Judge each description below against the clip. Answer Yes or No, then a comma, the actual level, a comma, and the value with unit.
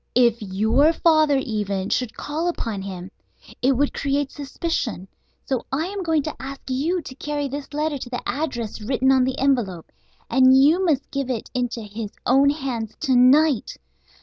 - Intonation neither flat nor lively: Yes, average, 3.9 semitones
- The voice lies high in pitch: Yes, very high, 265 Hz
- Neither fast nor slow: Yes, average, 175 wpm